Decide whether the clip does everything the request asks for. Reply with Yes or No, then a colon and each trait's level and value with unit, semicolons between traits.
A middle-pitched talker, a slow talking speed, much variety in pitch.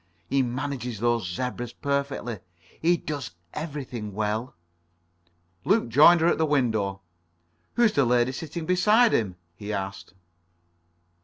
No: low, 125 Hz; slow, 130 wpm; wide, 5.7 semitones